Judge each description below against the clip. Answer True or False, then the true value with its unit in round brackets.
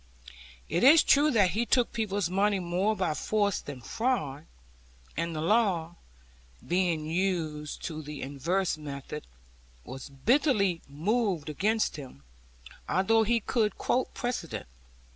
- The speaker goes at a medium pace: False (125 wpm)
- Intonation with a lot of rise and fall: True (6.0 semitones)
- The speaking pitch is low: False (185 Hz)